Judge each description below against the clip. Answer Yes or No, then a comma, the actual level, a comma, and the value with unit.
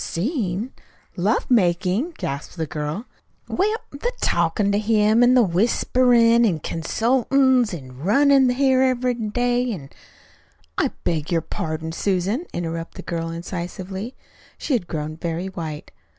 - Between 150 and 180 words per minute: No, slow, 135 wpm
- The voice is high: Yes, high, 205 Hz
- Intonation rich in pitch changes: Yes, wide, 6.7 semitones